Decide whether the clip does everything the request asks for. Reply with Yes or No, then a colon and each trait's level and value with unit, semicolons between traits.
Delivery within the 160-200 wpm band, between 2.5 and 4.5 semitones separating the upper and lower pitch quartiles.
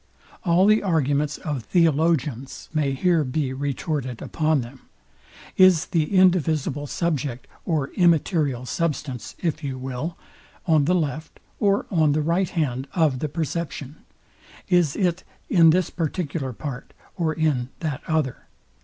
No: slow, 135 wpm; average, 3.6 semitones